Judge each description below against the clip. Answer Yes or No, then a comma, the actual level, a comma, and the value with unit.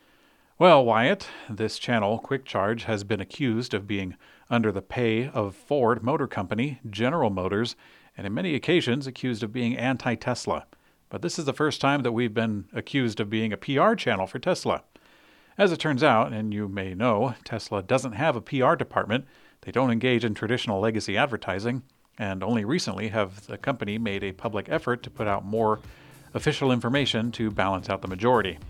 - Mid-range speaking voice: No, low, 115 Hz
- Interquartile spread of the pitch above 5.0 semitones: No, average, 3.5 semitones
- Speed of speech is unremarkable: Yes, average, 185 wpm